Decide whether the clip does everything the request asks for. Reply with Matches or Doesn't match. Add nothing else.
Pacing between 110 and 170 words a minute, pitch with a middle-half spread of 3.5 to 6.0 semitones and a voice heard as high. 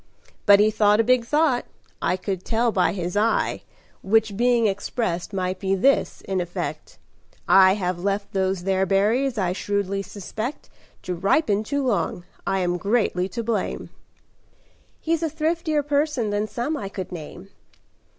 Matches